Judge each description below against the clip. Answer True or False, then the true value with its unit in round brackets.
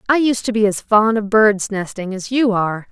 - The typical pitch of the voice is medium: False (210 Hz)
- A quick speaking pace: True (225 wpm)